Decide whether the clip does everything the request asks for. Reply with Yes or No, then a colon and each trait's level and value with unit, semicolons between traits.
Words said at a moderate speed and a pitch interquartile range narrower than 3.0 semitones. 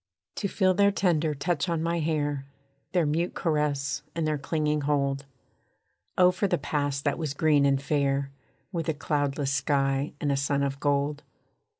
Yes: average, 170 wpm; narrow, 2.4 semitones